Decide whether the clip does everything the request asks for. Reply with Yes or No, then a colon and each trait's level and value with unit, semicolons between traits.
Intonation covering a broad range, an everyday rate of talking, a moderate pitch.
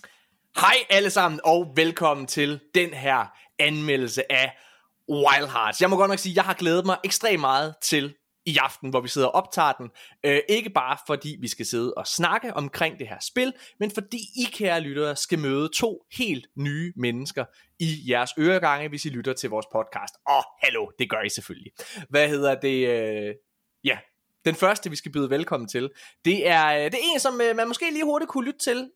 Yes: wide, 6.4 semitones; average, 205 wpm; medium, 155 Hz